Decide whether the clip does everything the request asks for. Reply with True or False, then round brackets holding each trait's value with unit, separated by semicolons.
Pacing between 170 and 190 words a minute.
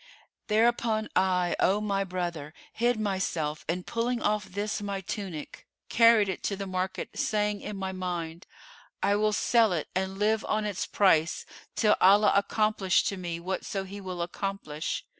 False (160 wpm)